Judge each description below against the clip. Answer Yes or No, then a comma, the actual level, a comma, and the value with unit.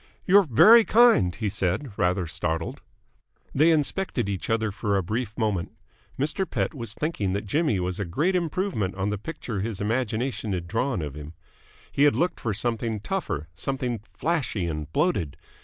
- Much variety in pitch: Yes, wide, 7.9 semitones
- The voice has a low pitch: Yes, low, 110 Hz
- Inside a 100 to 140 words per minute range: No, average, 170 wpm